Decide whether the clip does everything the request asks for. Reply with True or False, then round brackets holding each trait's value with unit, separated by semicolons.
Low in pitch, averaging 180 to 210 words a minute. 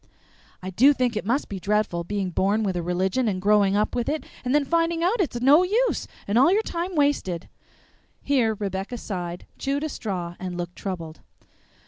False (215 Hz; 190 wpm)